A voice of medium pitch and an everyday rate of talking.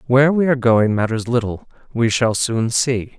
No: low, 120 Hz; average, 190 wpm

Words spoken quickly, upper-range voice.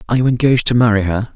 No: fast, 265 wpm; low, 115 Hz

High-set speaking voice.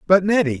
No: medium, 180 Hz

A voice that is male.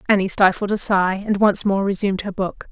No: female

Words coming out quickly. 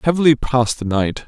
No: average, 190 wpm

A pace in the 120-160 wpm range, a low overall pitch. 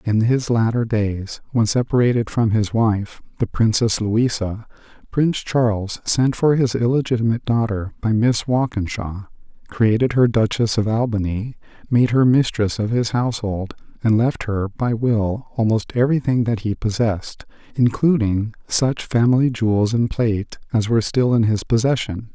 Yes: average, 150 wpm; low, 115 Hz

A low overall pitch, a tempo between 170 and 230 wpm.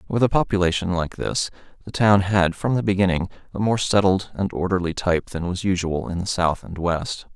Yes: very low, 95 Hz; fast, 205 wpm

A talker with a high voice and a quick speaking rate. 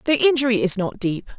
Yes: high, 225 Hz; fast, 215 wpm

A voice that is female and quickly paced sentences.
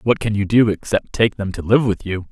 No: male; fast, 285 wpm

